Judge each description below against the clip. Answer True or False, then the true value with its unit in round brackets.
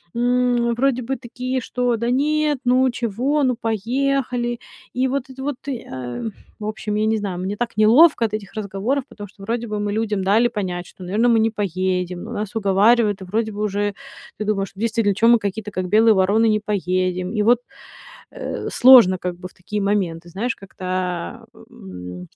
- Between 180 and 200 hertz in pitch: False (215 Hz)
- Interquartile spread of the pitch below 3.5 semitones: False (3.8 semitones)